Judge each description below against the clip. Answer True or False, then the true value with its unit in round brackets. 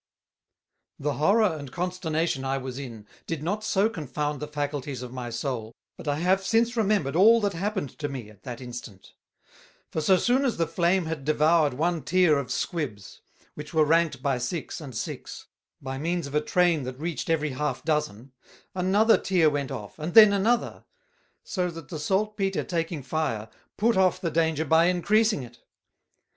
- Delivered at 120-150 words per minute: False (180 wpm)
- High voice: False (160 Hz)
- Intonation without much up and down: False (5.0 semitones)